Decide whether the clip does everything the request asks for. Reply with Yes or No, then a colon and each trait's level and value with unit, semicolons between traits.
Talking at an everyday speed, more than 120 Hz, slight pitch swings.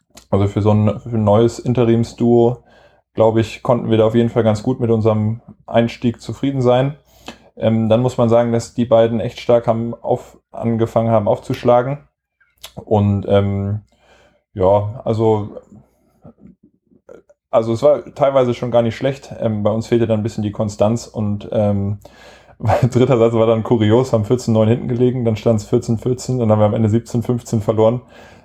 No: average, 175 wpm; low, 115 Hz; narrow, 1.7 semitones